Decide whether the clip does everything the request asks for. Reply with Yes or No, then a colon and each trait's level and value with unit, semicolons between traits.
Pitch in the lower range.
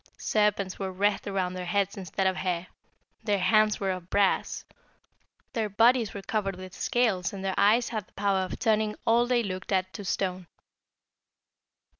No: high, 200 Hz